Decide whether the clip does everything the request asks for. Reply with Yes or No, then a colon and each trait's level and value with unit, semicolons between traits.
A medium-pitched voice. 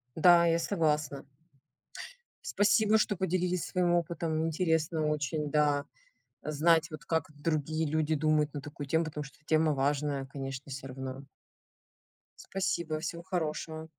Yes: medium, 155 Hz